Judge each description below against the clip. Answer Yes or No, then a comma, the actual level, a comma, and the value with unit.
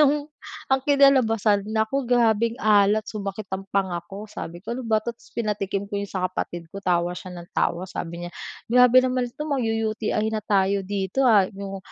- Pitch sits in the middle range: No, high, 215 Hz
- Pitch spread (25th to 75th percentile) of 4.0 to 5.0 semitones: No, average, 3.5 semitones